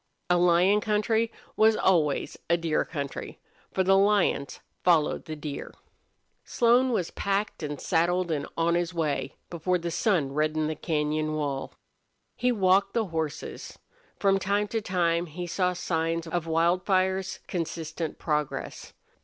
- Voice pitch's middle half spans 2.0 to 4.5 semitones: Yes, average, 3.6 semitones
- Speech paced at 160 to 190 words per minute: No, average, 140 wpm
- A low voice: No, medium, 175 Hz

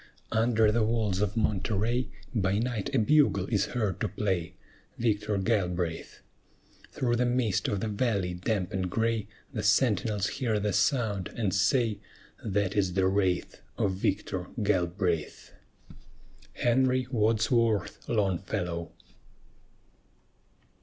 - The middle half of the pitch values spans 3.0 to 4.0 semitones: Yes, average, 3.3 semitones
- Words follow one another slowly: Yes, slow, 120 wpm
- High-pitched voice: No, low, 105 Hz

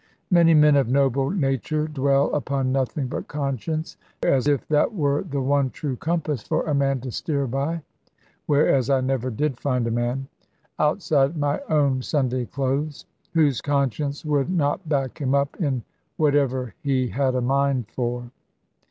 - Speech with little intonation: Yes, narrow, 2.2 semitones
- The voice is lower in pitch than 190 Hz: Yes, medium, 140 Hz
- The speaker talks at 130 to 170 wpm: Yes, average, 160 wpm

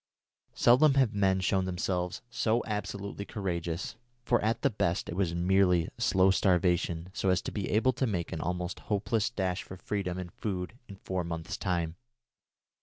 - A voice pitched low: Yes, very low, 95 Hz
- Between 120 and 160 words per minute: No, average, 170 wpm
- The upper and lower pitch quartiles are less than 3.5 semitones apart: Yes, average, 2.7 semitones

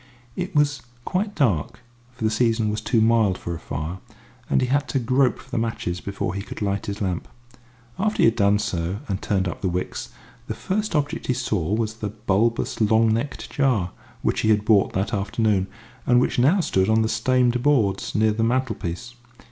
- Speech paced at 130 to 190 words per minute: No, average, 200 wpm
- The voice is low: Yes, low, 110 Hz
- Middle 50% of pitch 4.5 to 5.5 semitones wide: No, average, 4.1 semitones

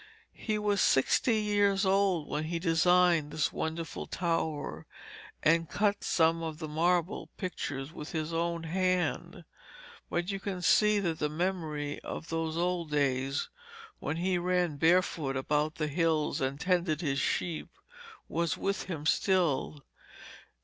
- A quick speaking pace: No, average, 140 wpm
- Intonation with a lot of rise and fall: No, average, 3.0 semitones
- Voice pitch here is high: No, medium, 165 Hz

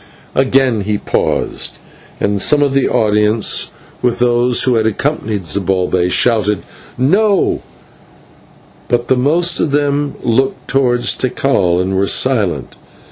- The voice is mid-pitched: No, low, 120 Hz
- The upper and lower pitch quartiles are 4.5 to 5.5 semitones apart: Yes, average, 4.8 semitones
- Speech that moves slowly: Yes, slow, 125 wpm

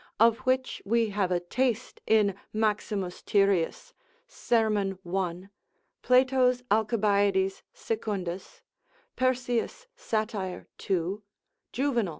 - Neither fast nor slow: No, slow, 90 wpm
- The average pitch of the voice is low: No, high, 215 Hz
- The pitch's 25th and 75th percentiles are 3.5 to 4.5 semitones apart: Yes, average, 3.8 semitones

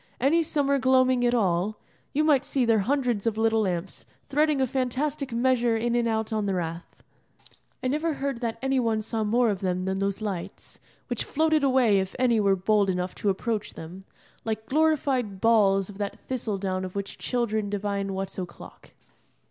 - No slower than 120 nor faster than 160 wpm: No, average, 180 wpm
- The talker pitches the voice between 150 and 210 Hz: No, high, 225 Hz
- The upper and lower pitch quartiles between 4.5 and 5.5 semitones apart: Yes, average, 4.8 semitones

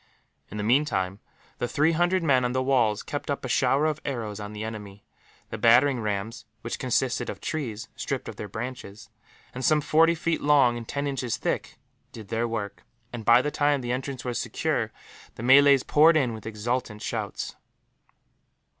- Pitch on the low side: Yes, low, 125 Hz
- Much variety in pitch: No, average, 4.5 semitones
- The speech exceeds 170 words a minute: Yes, average, 180 wpm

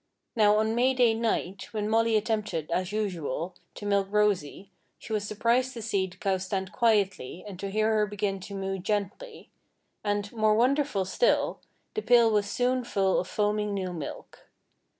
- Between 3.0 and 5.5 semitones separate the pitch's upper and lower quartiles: No, narrow, 2.6 semitones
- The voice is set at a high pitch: Yes, high, 210 Hz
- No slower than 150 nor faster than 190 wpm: Yes, average, 170 wpm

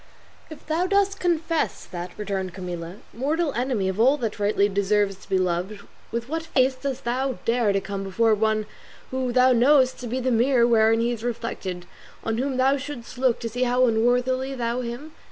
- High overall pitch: Yes, high, 240 Hz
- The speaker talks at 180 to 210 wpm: Yes, average, 190 wpm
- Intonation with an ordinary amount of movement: Yes, average, 3.8 semitones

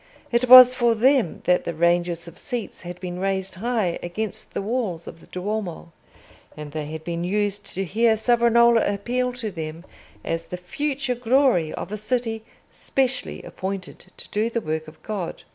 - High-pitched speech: Yes, high, 205 Hz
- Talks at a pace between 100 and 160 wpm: No, average, 175 wpm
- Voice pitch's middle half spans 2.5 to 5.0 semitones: No, wide, 5.4 semitones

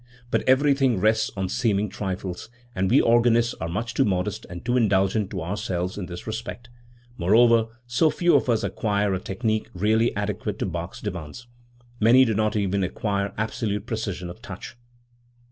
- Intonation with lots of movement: No, average, 3.6 semitones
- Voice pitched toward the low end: Yes, low, 105 Hz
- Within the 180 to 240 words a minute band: No, average, 165 wpm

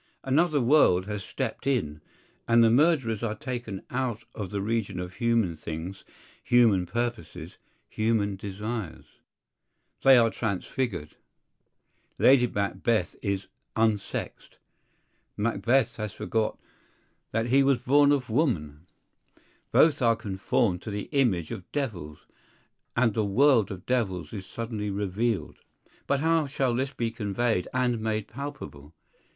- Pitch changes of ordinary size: Yes, average, 4.3 semitones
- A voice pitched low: Yes, low, 110 Hz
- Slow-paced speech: Yes, slow, 125 wpm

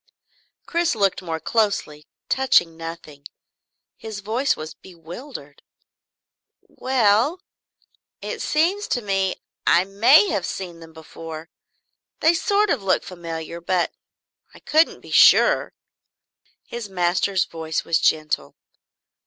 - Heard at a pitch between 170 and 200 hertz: Yes, high, 190 Hz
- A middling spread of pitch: No, wide, 6.3 semitones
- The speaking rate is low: Yes, slow, 110 wpm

